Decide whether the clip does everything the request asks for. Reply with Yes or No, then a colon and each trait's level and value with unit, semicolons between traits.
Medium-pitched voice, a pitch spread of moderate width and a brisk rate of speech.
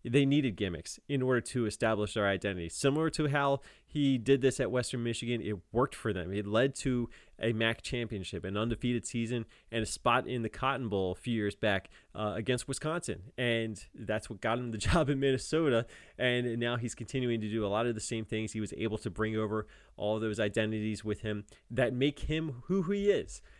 No: low, 115 Hz; average, 3.2 semitones; fast, 215 wpm